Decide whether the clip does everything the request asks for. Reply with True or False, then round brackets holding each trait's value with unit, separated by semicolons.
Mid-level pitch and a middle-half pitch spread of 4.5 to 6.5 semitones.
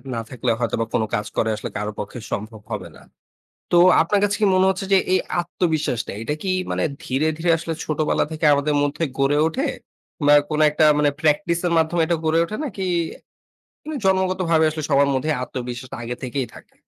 True (155 Hz; 5.2 semitones)